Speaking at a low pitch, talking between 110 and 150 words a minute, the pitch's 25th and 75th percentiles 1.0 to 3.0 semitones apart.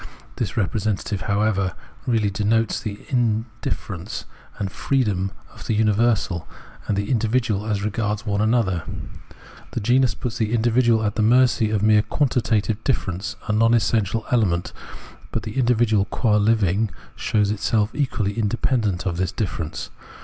Yes: low, 110 Hz; average, 145 wpm; narrow, 2.4 semitones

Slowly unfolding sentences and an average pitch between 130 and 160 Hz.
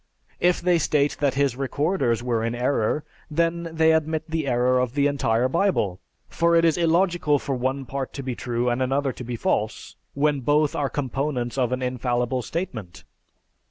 No: average, 180 wpm; medium, 140 Hz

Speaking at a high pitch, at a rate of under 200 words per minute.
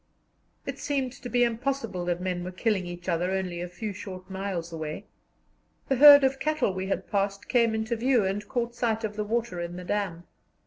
No: high, 205 Hz; fast, 205 wpm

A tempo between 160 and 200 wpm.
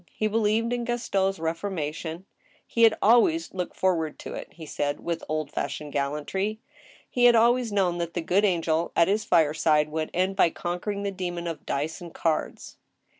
Yes: average, 175 wpm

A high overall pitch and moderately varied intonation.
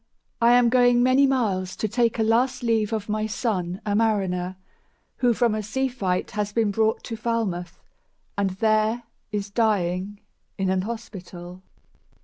Yes: high, 215 Hz; average, 3.5 semitones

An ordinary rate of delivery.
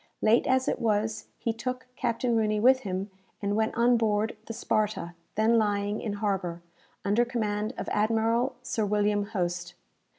Yes: average, 160 wpm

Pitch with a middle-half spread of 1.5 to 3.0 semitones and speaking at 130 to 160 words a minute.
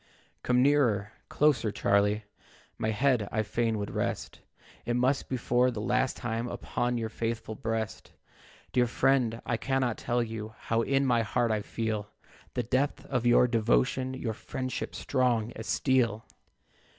Yes: narrow, 2.5 semitones; average, 150 wpm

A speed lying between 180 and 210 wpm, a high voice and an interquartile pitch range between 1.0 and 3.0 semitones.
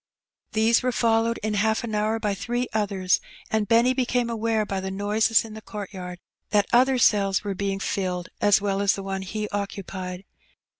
Yes: average, 195 wpm; high, 210 Hz; narrow, 2.4 semitones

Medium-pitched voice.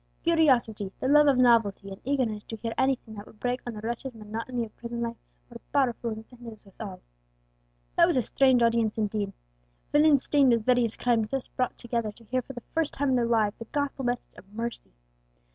No: high, 235 Hz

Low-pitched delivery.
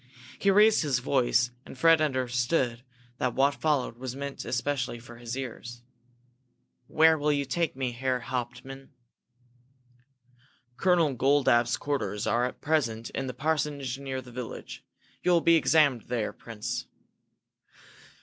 Yes: low, 130 Hz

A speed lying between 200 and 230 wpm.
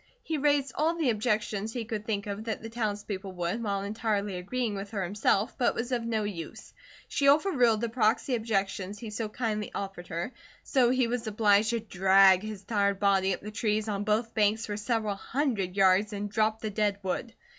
Yes: fast, 205 wpm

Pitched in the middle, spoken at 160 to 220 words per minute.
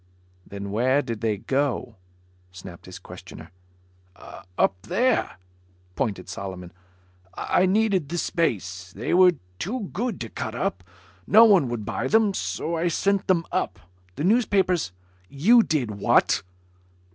No: medium, 145 Hz; slow, 135 wpm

